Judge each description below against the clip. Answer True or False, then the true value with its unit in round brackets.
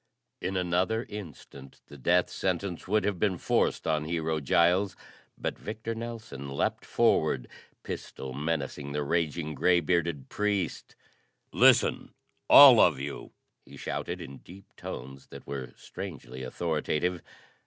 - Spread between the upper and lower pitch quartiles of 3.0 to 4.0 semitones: False (4.9 semitones)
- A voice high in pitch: False (85 Hz)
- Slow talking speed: True (130 wpm)